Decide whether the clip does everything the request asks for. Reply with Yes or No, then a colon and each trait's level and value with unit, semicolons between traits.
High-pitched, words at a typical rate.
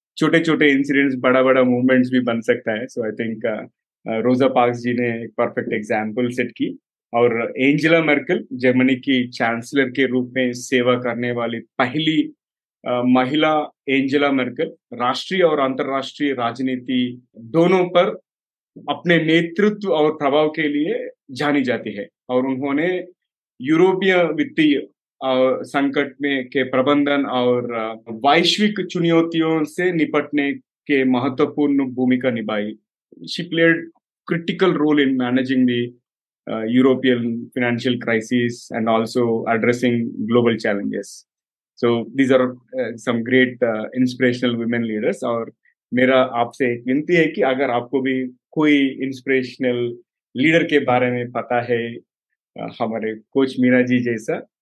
No: low, 130 Hz; average, 125 wpm